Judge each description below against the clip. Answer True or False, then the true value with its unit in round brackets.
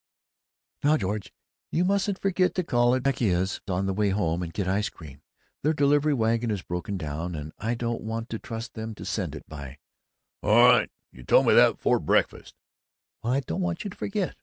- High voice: False (115 Hz)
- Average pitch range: False (7.0 semitones)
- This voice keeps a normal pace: False (215 wpm)